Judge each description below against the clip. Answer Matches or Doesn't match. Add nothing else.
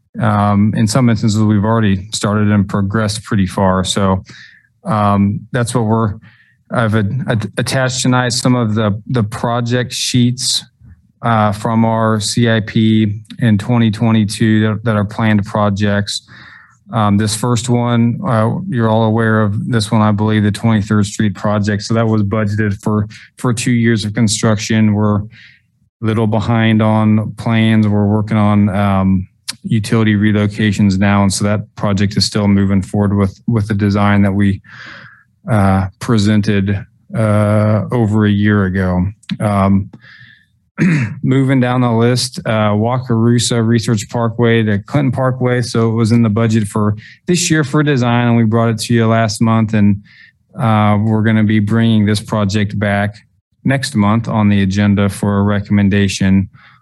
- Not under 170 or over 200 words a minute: Doesn't match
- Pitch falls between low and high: Doesn't match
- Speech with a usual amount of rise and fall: Doesn't match